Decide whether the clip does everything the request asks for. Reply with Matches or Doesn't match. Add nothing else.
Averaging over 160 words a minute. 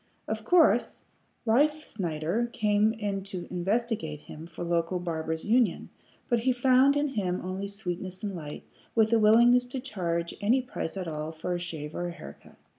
Matches